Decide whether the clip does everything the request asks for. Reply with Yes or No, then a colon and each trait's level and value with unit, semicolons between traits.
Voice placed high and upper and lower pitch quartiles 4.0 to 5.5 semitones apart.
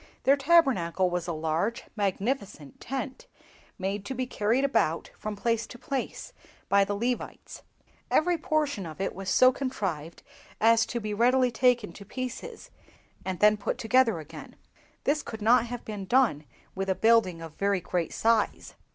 Yes: high, 220 Hz; average, 5.0 semitones